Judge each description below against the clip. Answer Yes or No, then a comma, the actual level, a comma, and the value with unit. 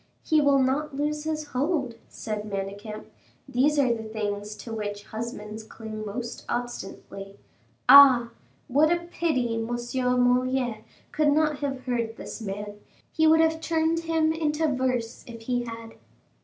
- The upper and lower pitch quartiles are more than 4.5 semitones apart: Yes, average, 5.2 semitones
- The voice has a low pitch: No, high, 245 Hz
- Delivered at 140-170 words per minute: Yes, average, 145 wpm